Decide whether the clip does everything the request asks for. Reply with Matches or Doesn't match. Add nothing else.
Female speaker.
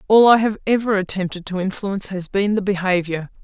Matches